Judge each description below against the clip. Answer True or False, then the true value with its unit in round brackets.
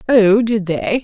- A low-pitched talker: False (210 Hz)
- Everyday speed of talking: True (175 wpm)